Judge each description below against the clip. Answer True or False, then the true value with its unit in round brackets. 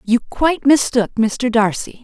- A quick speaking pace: False (145 wpm)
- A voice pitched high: True (240 Hz)